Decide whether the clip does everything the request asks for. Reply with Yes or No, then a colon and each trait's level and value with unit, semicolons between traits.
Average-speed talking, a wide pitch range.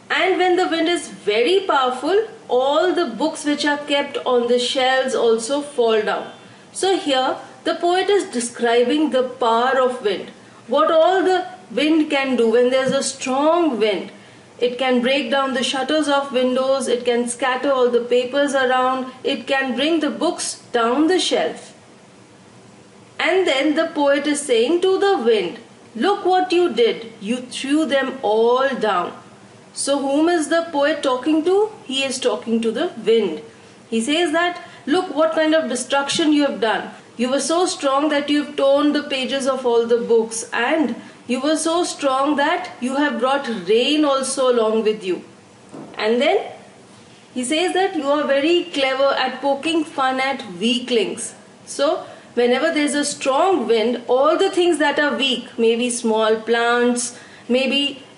No: average, 170 wpm; average, 4.6 semitones